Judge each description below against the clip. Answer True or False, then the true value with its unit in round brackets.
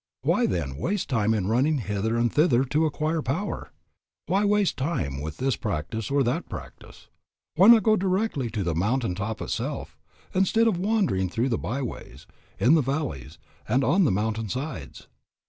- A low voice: True (130 Hz)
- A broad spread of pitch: True (8.0 semitones)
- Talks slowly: False (175 wpm)